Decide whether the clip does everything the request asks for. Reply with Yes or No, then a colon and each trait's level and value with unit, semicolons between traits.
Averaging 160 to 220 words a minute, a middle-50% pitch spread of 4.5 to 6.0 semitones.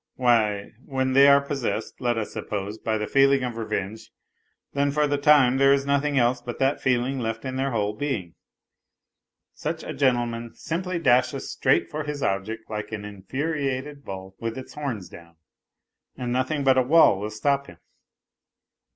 No: average, 170 wpm; average, 4.0 semitones